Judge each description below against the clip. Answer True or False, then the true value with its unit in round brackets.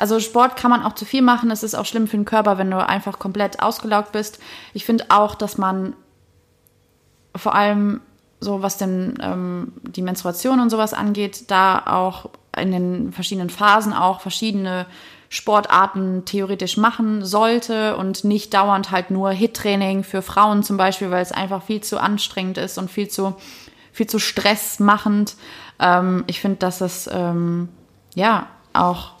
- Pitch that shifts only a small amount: True (2.0 semitones)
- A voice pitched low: False (205 Hz)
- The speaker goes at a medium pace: True (165 wpm)